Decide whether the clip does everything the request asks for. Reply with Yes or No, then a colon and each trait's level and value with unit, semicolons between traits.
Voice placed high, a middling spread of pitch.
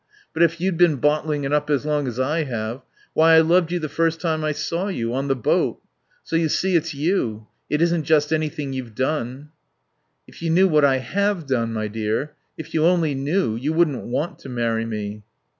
No: medium, 150 Hz; average, 4.1 semitones